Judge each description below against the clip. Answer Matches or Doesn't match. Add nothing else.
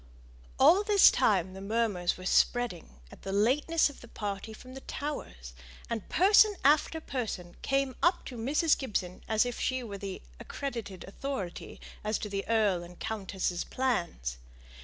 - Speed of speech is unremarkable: Matches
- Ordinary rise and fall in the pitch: Doesn't match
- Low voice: Doesn't match